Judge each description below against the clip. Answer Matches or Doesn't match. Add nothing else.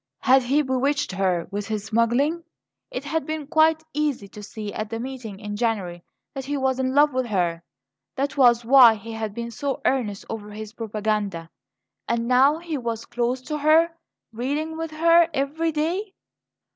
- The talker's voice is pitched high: Matches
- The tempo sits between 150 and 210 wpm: Matches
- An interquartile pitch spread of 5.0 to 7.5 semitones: Matches